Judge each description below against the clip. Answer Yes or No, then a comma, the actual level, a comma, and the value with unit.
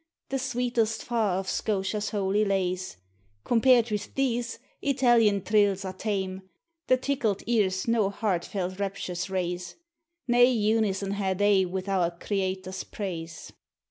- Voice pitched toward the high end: Yes, high, 200 Hz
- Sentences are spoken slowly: Yes, slow, 125 wpm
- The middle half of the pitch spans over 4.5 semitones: No, average, 3.4 semitones